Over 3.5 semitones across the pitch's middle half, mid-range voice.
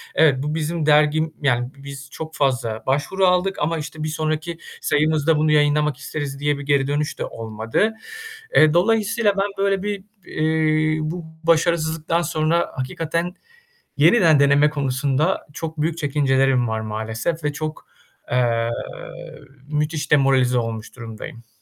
No: average, 2.9 semitones; medium, 150 Hz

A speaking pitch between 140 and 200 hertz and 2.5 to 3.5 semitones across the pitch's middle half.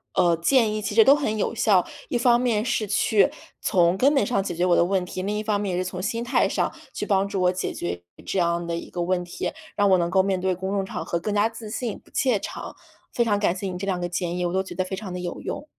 Yes: high, 190 Hz; average, 3.2 semitones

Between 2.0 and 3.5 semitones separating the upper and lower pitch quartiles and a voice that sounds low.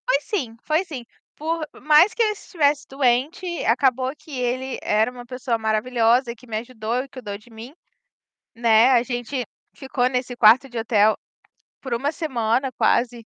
No: average, 3.1 semitones; very high, 250 Hz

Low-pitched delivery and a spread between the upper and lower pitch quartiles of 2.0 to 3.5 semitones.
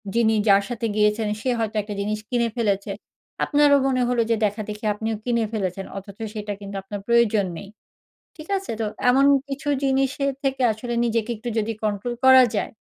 No: high, 225 Hz; average, 3.2 semitones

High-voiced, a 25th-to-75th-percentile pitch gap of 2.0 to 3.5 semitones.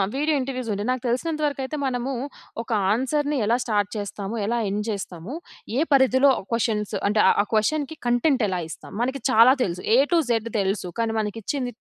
No: high, 240 Hz; average, 4.4 semitones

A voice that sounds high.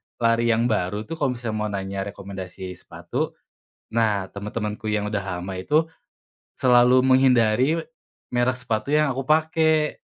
No: low, 115 Hz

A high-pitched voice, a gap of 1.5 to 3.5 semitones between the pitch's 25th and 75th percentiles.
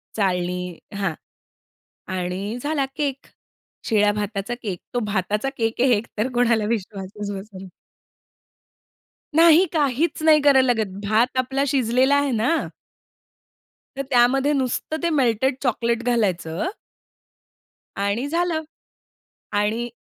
No: high, 235 Hz; average, 4.9 semitones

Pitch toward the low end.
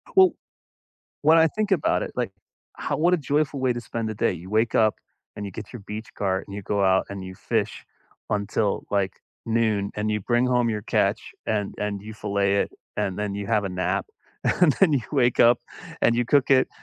Yes: low, 110 Hz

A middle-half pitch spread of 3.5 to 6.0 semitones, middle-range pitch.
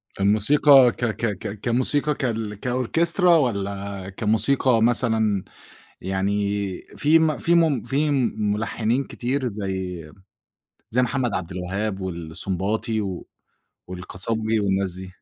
No: average, 4.6 semitones; low, 110 Hz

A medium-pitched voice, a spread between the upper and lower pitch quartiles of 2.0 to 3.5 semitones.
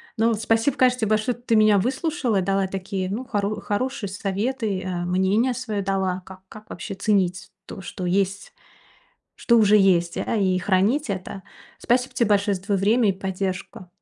No: high, 200 Hz; average, 3.2 semitones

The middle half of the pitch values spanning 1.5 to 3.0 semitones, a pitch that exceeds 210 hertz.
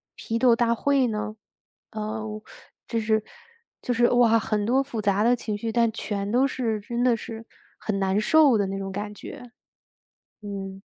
Yes: narrow, 2.5 semitones; high, 220 Hz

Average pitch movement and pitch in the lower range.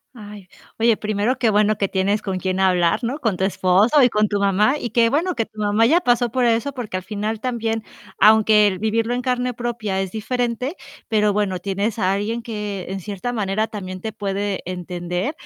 No: average, 3.3 semitones; high, 215 Hz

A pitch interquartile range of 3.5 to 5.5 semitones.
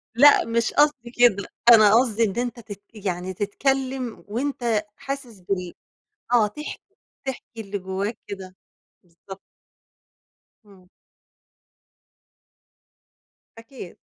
Yes: average, 4.5 semitones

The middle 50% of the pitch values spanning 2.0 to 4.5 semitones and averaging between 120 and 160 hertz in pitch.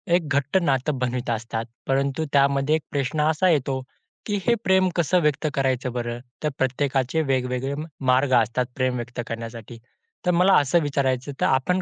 Yes: average, 3.2 semitones; low, 135 Hz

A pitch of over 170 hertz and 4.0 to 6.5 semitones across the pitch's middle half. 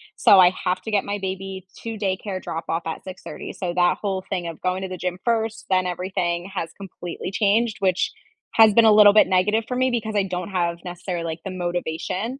No: high, 190 Hz; average, 2.8 semitones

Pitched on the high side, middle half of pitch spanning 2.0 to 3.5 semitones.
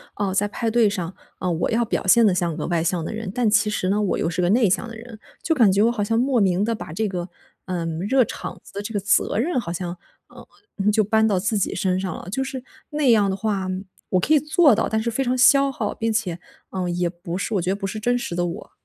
No: high, 210 Hz; average, 4.1 semitones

